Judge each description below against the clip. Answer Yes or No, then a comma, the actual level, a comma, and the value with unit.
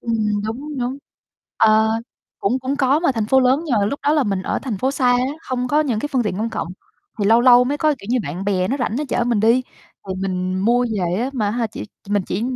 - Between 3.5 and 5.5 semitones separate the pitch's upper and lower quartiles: Yes, average, 4.2 semitones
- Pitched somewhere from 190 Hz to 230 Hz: No, high, 240 Hz